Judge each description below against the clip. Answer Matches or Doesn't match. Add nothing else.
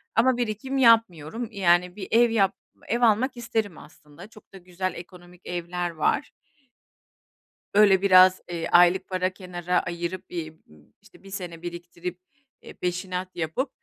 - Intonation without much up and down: Doesn't match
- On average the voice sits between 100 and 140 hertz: Doesn't match